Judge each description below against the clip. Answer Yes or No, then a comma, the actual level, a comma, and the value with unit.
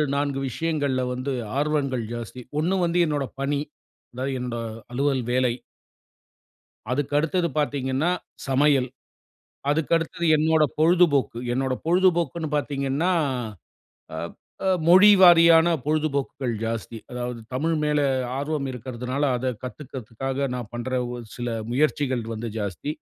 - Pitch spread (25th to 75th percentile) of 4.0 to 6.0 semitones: No, average, 3.6 semitones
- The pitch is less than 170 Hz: Yes, medium, 140 Hz